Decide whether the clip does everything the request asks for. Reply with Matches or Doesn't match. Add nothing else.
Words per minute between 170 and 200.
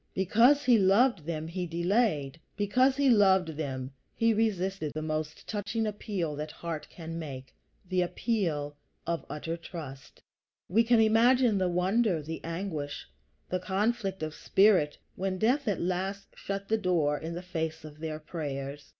Doesn't match